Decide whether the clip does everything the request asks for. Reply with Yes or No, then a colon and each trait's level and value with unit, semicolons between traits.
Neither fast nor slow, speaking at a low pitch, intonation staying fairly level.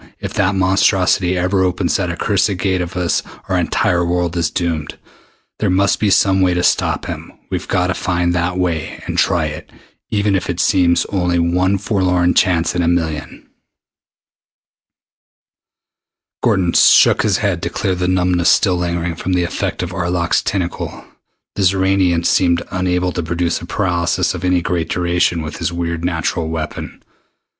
Yes: average, 165 wpm; very low, 90 Hz; narrow, 1.3 semitones